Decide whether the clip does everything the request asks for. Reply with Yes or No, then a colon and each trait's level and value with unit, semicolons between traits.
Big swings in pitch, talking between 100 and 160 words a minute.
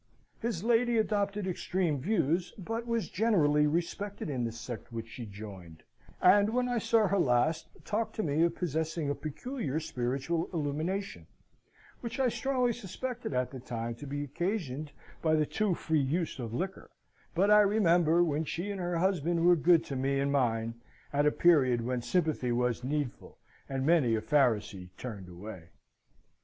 No: wide, 7.2 semitones; average, 170 wpm